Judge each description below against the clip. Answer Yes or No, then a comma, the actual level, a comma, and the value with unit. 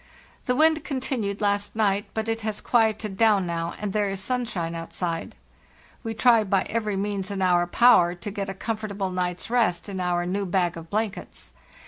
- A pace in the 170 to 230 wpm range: Yes, average, 185 wpm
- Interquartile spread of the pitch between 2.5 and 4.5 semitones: Yes, average, 3.4 semitones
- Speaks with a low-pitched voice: No, high, 200 Hz